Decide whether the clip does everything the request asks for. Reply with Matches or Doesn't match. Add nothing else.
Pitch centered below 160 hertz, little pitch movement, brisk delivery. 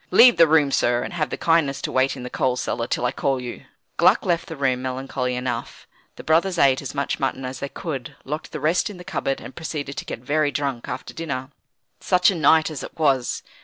Doesn't match